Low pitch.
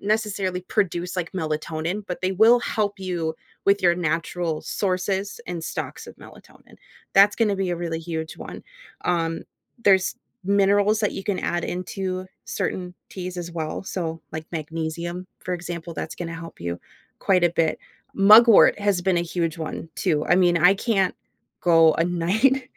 No: medium, 180 Hz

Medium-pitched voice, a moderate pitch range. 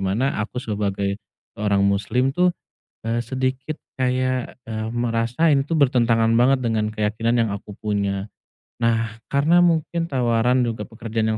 No: low, 115 Hz; average, 3.1 semitones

